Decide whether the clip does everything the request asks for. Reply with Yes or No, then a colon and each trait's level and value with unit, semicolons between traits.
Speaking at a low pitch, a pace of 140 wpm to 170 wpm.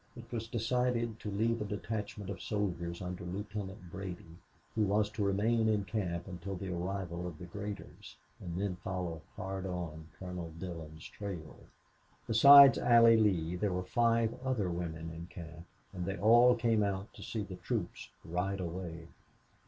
Yes: very low, 95 Hz; average, 160 wpm